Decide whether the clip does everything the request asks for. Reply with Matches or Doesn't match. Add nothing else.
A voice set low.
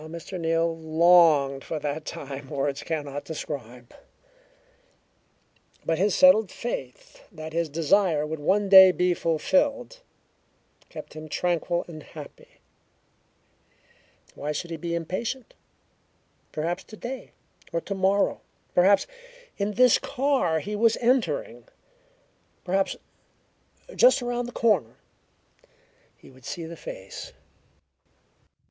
Doesn't match